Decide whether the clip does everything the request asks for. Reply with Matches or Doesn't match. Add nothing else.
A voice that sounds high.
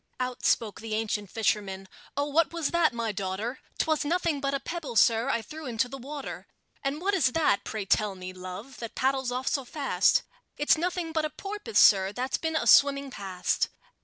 Matches